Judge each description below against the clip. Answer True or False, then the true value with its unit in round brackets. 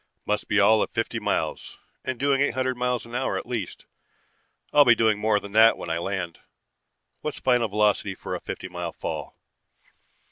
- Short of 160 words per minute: False (185 wpm)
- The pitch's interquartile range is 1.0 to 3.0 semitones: False (3.6 semitones)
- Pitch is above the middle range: False (110 Hz)